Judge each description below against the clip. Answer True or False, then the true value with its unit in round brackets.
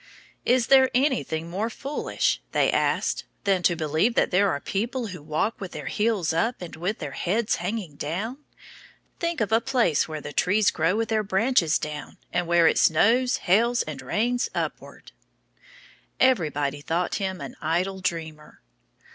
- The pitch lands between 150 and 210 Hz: True (190 Hz)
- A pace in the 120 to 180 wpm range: True (165 wpm)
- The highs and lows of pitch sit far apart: True (6.0 semitones)